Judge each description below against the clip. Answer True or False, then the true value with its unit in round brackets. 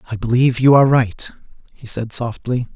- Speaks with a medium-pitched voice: False (120 Hz)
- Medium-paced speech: True (175 wpm)